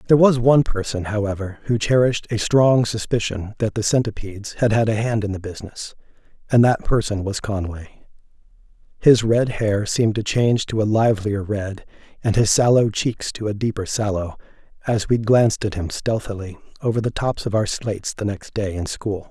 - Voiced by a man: Yes, male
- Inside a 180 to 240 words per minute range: Yes, average, 185 wpm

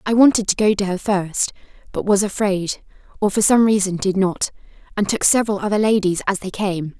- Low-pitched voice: No, high, 200 Hz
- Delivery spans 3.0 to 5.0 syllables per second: No, 5.5 syllables/s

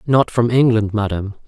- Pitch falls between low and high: No, low, 110 Hz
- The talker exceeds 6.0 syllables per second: No, 5.6 syllables/s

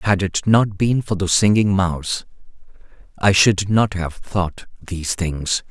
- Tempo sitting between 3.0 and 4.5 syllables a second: Yes, 4.1 syllables/s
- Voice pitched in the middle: No, very low, 95 Hz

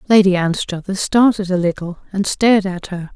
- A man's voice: No, female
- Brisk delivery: No, average, 170 wpm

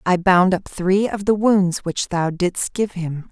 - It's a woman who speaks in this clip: Yes, female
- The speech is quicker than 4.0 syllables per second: No, 3.8 syllables/s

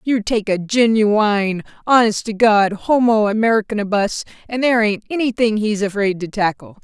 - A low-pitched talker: No, high, 215 Hz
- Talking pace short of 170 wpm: Yes, average, 150 wpm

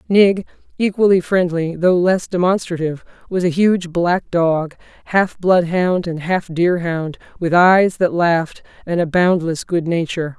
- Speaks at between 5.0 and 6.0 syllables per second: No, 4.3 syllables/s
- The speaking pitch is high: No, medium, 175 Hz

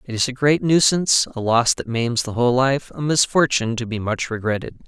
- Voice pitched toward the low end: Yes, low, 125 Hz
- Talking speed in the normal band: No, fast, 210 wpm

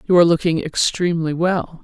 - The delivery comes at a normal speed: Yes, average, 165 wpm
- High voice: No, medium, 170 Hz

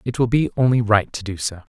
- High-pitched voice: No, low, 115 Hz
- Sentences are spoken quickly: Yes, fast, 275 wpm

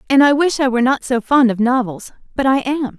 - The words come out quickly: Yes, fast, 260 wpm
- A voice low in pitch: No, very high, 255 Hz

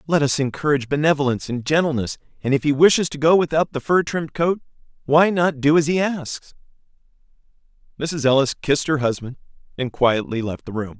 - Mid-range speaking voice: Yes, medium, 145 Hz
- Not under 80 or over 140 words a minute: No, average, 180 wpm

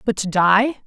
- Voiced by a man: No, female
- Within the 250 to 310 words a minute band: No, fast, 210 wpm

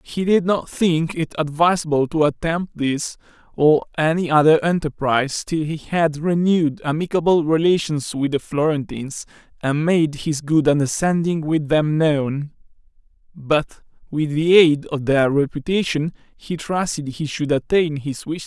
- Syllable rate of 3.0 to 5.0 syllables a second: Yes, 4.5 syllables/s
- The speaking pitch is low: No, medium, 155 Hz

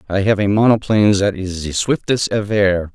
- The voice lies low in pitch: Yes, low, 100 Hz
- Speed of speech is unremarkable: Yes, average, 185 wpm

